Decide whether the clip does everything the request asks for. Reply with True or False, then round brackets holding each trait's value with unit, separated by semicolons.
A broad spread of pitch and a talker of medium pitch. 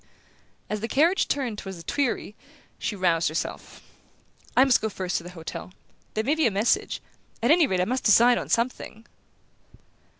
False (5.7 semitones; 220 Hz)